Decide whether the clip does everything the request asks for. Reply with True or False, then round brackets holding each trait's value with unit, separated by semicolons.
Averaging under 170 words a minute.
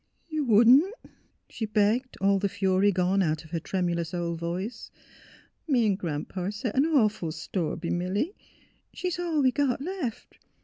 False (190 wpm)